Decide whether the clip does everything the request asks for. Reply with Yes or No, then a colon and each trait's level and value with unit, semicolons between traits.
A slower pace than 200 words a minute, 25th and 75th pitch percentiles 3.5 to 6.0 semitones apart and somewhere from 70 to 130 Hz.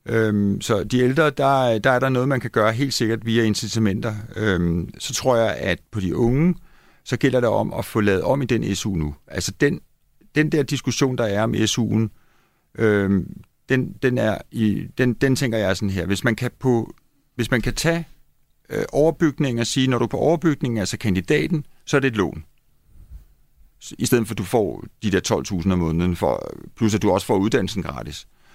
No: average, 210 wpm; average, 4.5 semitones; low, 115 Hz